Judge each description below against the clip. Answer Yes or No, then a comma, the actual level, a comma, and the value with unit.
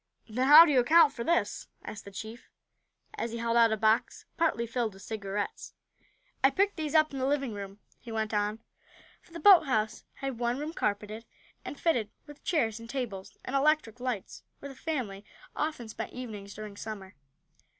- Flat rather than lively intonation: No, average, 5.0 semitones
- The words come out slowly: No, average, 185 wpm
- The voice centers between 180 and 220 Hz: No, high, 235 Hz